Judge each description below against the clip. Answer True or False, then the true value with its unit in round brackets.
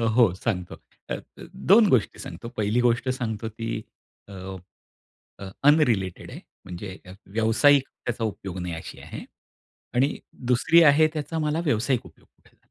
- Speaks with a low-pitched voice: True (115 Hz)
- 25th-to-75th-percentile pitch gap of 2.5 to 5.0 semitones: False (6.0 semitones)